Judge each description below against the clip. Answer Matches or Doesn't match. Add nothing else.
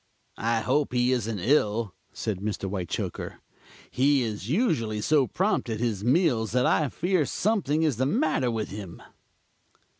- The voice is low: Matches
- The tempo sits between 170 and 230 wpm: Doesn't match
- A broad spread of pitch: Matches